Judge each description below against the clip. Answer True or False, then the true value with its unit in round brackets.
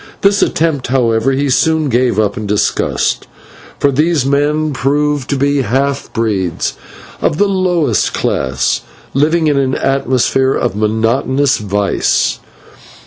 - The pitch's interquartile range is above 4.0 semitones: True (4.4 semitones)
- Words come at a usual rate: False (130 wpm)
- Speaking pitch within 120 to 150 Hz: True (135 Hz)